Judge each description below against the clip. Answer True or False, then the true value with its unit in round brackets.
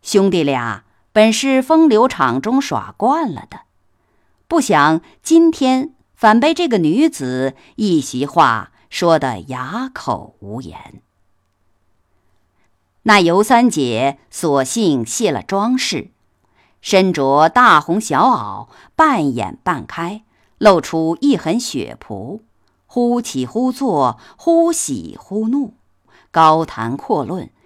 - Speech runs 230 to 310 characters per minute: False (150 characters per minute)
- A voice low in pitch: False (175 Hz)